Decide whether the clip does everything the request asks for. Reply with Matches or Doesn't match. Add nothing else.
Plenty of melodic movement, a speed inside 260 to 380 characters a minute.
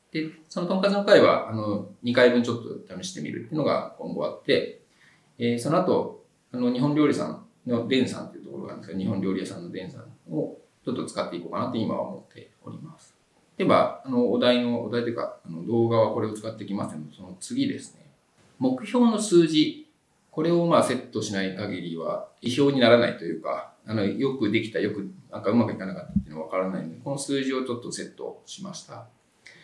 Doesn't match